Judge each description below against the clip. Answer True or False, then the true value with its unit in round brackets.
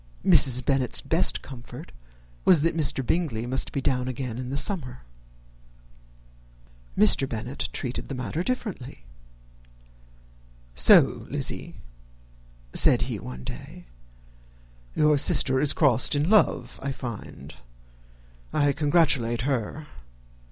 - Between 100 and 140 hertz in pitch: True (135 Hz)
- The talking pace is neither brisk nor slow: False (110 wpm)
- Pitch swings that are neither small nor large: True (3.4 semitones)